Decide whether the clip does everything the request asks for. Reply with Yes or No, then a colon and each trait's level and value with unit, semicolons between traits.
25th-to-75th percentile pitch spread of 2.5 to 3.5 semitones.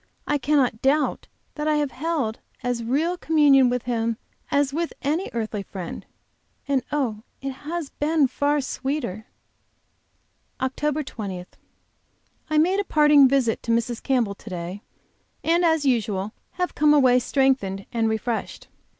No: average, 4.7 semitones